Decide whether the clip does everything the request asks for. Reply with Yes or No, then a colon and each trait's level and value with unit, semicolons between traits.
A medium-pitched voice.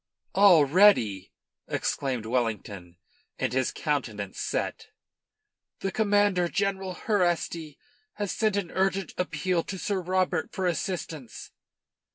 Yes: medium, 180 Hz